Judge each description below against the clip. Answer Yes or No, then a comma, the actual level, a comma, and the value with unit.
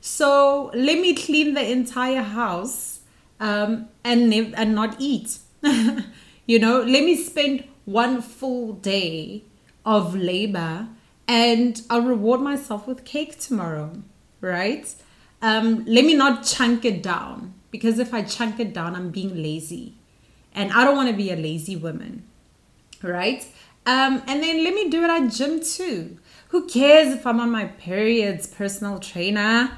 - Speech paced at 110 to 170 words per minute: Yes, average, 155 wpm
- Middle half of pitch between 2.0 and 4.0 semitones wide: No, average, 4.5 semitones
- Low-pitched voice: No, high, 235 Hz